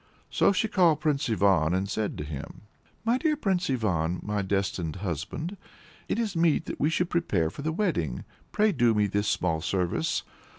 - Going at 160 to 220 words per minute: Yes, average, 180 wpm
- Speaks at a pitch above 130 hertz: No, low, 110 Hz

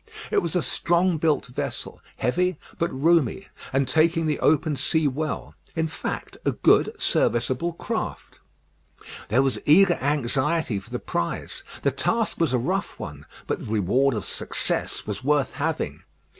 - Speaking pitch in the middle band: Yes, medium, 150 Hz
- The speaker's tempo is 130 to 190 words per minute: Yes, average, 155 wpm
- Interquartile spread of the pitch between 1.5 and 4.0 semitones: No, average, 4.4 semitones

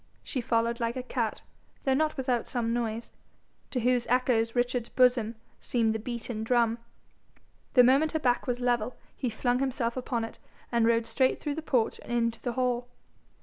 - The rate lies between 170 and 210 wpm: Yes, average, 180 wpm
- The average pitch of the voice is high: Yes, high, 245 Hz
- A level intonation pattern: Yes, narrow, 1.5 semitones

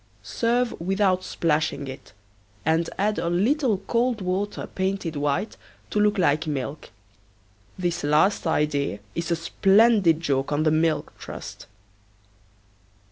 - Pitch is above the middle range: No, medium, 170 Hz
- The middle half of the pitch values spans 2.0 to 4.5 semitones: No, average, 5.0 semitones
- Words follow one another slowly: Yes, slow, 125 wpm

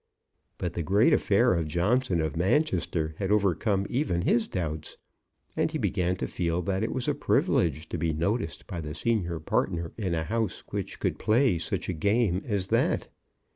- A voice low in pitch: Yes, very low, 90 Hz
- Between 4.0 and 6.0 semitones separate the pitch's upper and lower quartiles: Yes, average, 4.4 semitones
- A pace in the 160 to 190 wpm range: Yes, average, 180 wpm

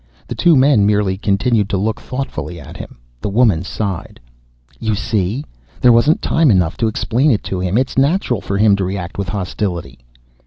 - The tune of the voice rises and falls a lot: No, average, 4.3 semitones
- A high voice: No, low, 105 Hz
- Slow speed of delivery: No, average, 185 wpm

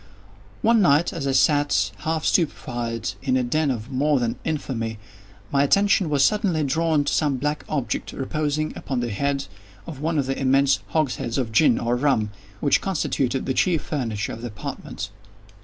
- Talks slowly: No, average, 175 wpm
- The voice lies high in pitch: No, medium, 140 Hz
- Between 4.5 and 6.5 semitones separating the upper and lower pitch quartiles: No, average, 3.9 semitones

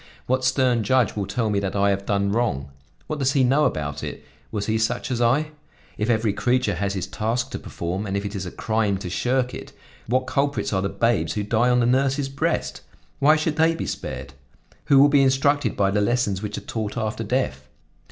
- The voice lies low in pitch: Yes, low, 115 Hz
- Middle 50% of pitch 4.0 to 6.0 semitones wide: Yes, average, 4.6 semitones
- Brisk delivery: Yes, fast, 220 wpm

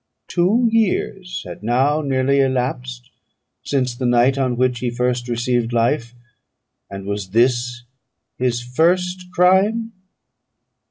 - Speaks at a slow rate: Yes, slow, 115 wpm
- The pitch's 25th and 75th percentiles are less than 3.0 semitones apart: No, wide, 5.5 semitones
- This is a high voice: No, low, 125 Hz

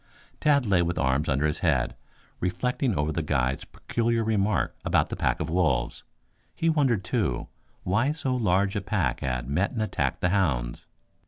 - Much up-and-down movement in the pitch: Yes, wide, 7.3 semitones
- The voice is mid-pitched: No, very low, 90 Hz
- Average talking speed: Yes, average, 170 wpm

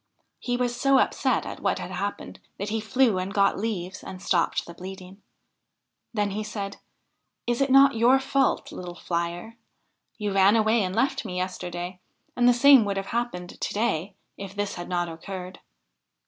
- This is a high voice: Yes, high, 200 Hz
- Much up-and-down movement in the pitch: No, average, 4.5 semitones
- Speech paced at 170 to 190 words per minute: Yes, average, 175 wpm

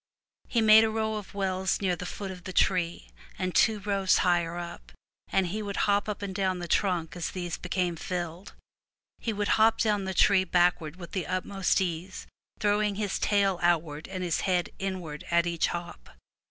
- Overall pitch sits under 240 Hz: Yes, medium, 185 Hz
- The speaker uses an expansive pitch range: No, narrow, 2.6 semitones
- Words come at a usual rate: Yes, average, 190 wpm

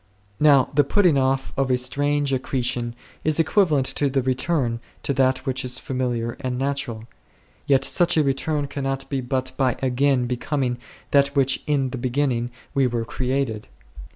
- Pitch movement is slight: Yes, narrow, 2.0 semitones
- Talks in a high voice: No, low, 135 Hz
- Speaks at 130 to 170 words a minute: Yes, average, 165 wpm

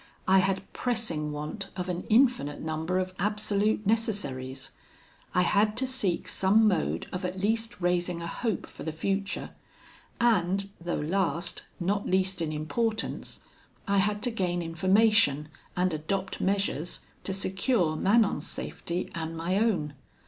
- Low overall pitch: No, high, 190 Hz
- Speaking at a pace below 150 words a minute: Yes, average, 140 wpm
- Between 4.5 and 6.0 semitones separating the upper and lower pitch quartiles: No, average, 3.8 semitones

